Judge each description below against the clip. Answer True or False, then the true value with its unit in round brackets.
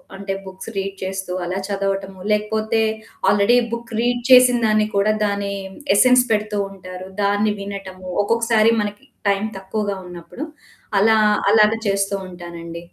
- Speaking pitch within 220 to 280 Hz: False (200 Hz)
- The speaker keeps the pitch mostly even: True (2.1 semitones)